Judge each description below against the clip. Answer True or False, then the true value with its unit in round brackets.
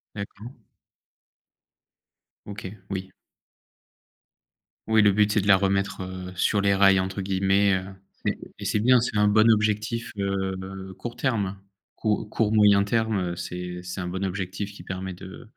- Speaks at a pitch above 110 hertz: False (100 Hz)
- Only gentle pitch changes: True (1.9 semitones)